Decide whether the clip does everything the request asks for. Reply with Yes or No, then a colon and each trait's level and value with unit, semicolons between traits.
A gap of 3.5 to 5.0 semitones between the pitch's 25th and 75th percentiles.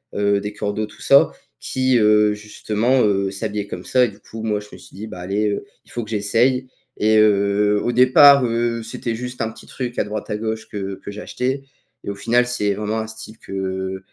No: average, 2.7 semitones